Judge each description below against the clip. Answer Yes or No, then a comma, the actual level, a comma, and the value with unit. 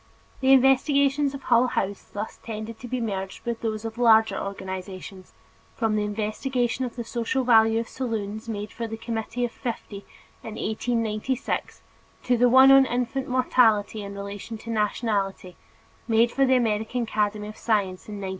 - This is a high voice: Yes, high, 225 Hz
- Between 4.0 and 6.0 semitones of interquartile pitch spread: No, average, 2.9 semitones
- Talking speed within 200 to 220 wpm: No, average, 165 wpm